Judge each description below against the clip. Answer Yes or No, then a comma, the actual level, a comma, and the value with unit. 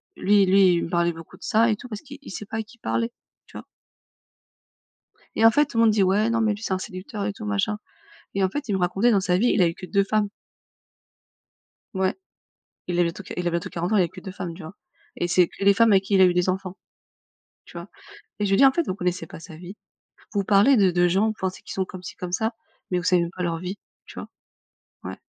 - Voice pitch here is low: No, high, 195 Hz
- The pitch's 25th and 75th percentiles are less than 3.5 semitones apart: Yes, average, 3.1 semitones